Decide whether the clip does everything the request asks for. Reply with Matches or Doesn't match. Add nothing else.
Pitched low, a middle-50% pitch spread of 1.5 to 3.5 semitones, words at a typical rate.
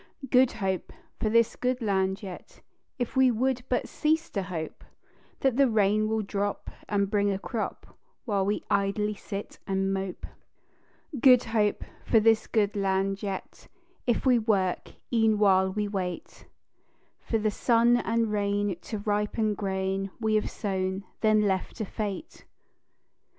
Doesn't match